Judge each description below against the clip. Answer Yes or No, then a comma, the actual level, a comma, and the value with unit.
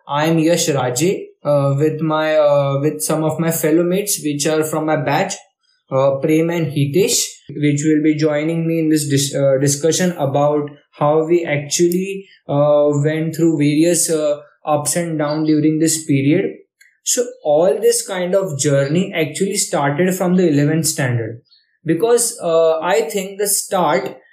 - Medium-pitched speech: Yes, medium, 155 Hz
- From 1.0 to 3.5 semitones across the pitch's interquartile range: Yes, average, 2.9 semitones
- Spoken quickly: No, average, 165 wpm